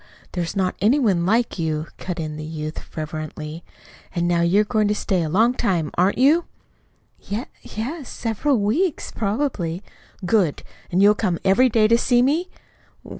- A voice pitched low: No, high, 200 Hz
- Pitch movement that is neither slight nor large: No, wide, 5.7 semitones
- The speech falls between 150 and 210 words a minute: Yes, average, 165 wpm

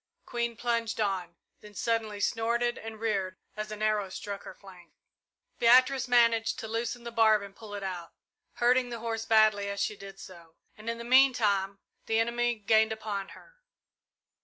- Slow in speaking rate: No, average, 170 wpm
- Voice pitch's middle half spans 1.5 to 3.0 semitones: Yes, average, 2.7 semitones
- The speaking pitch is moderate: No, high, 220 Hz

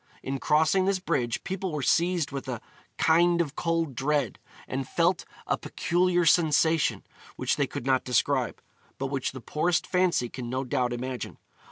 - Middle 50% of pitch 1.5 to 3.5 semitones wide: No, average, 4.8 semitones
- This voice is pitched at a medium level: Yes, medium, 150 Hz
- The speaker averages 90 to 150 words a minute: No, average, 165 wpm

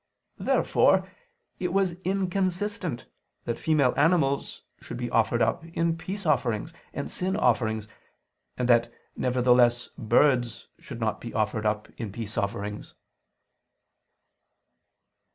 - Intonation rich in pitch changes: Yes, wide, 7.3 semitones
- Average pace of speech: No, slow, 115 wpm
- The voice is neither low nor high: No, low, 125 Hz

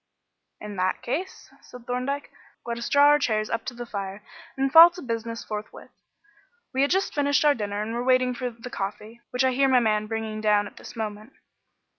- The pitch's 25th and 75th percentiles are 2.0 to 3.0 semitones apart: No, average, 3.8 semitones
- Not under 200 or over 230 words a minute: Yes, fast, 205 wpm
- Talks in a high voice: Yes, high, 235 Hz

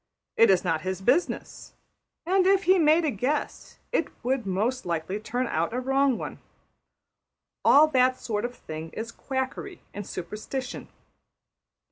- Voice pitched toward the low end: No, very high, 250 Hz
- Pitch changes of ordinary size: No, wide, 6.2 semitones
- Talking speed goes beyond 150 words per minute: No, average, 145 wpm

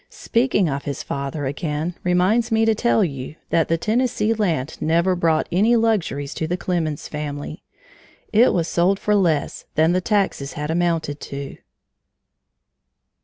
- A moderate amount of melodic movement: No, wide, 5.7 semitones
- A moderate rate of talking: Yes, average, 150 wpm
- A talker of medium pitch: Yes, medium, 170 Hz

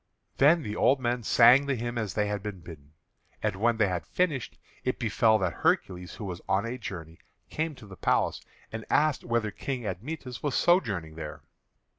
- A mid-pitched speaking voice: No, low, 110 Hz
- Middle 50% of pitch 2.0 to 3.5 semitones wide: No, average, 5.1 semitones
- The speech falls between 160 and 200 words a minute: Yes, average, 190 wpm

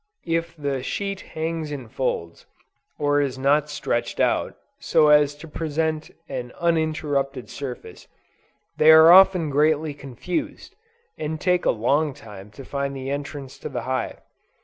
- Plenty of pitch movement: No, average, 2.8 semitones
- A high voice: No, medium, 145 Hz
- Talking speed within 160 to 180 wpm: No, average, 145 wpm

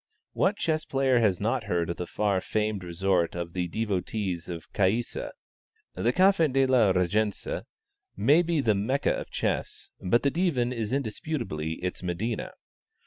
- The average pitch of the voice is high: No, low, 110 Hz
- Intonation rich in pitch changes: Yes, wide, 6.4 semitones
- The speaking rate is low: No, average, 155 wpm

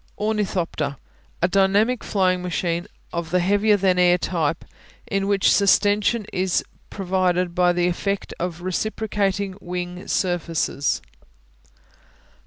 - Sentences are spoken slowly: Yes, slow, 110 wpm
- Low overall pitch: No, medium, 185 Hz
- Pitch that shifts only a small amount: Yes, narrow, 2.1 semitones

